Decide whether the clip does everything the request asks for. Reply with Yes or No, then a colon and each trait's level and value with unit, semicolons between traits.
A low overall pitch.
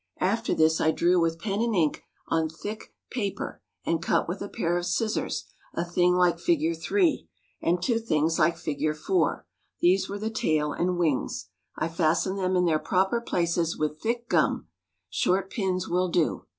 No: medium, 175 Hz